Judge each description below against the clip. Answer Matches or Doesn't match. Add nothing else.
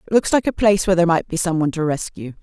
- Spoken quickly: Matches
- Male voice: Doesn't match